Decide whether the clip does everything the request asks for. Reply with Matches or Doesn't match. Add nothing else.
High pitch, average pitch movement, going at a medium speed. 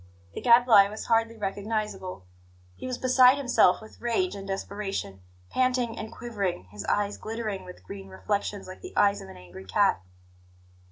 Matches